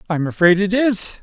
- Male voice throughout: Yes, male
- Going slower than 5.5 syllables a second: Yes, 5.3 syllables/s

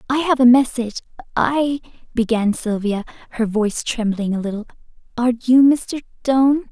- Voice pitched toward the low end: No, high, 240 Hz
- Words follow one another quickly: No, average, 145 wpm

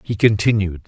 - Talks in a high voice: No, low, 105 Hz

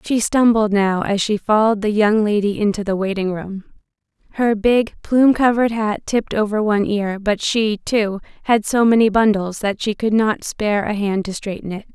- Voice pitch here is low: No, high, 210 Hz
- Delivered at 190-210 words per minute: Yes, average, 195 wpm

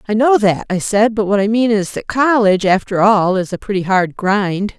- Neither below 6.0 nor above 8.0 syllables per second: No, 5.1 syllables/s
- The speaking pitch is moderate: No, high, 205 Hz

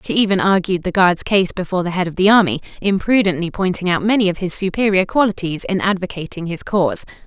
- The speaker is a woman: Yes, female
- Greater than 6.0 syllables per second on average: Yes, 6.2 syllables/s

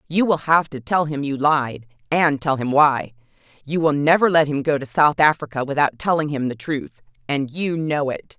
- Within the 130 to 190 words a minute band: No, average, 200 wpm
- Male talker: No, female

